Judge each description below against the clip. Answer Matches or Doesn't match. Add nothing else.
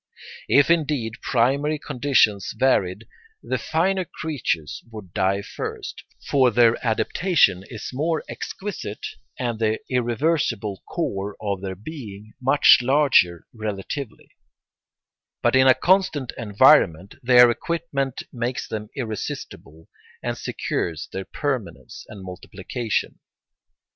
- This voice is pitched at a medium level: Doesn't match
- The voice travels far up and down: Matches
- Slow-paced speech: Matches